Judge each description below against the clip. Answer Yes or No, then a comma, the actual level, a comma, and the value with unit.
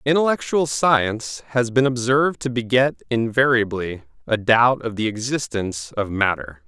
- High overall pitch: No, low, 120 Hz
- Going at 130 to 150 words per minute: Yes, slow, 135 wpm